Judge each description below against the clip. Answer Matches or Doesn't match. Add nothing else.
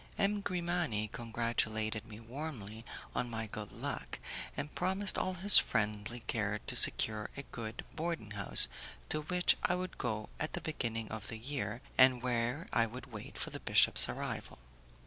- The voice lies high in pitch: Doesn't match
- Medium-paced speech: Matches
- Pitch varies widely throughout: Matches